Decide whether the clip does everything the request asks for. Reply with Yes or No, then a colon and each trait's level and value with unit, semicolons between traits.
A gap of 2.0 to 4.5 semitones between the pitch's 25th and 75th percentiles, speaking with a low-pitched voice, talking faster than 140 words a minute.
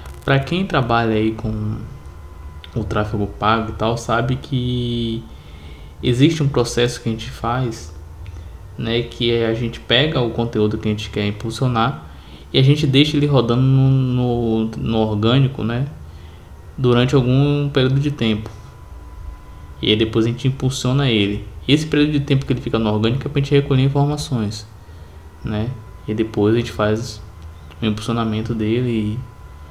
Yes: average, 3.6 semitones; low, 115 Hz; average, 160 wpm